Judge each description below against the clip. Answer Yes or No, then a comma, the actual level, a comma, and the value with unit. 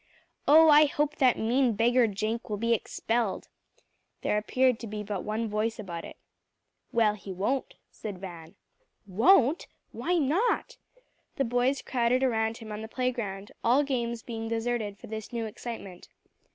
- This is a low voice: No, high, 230 Hz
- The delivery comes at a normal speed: Yes, average, 155 wpm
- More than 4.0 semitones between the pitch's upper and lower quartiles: No, average, 3.2 semitones